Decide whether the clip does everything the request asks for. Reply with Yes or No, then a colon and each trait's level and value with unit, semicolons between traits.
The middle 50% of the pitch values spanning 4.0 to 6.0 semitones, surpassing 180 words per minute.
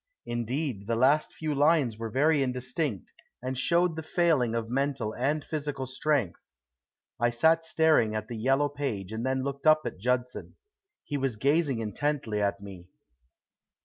No: average, 4.5 semitones; average, 155 wpm